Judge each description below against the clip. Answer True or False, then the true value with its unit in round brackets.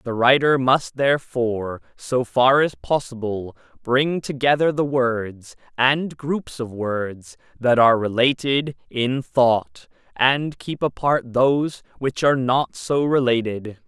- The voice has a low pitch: True (125 Hz)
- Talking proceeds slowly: True (130 wpm)